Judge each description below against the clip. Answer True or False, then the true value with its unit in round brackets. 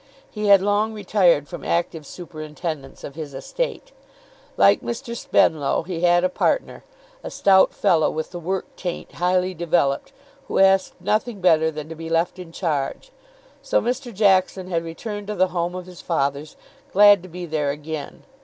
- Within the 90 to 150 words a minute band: False (170 wpm)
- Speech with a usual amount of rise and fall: True (3.5 semitones)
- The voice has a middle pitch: True (175 Hz)